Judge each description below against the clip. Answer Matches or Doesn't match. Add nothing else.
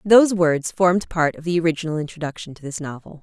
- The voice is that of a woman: Matches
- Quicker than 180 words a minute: Matches